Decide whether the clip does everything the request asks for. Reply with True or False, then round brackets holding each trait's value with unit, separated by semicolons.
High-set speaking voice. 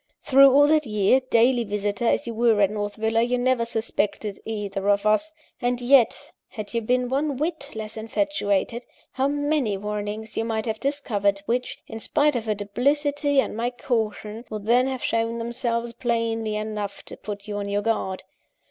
True (230 Hz)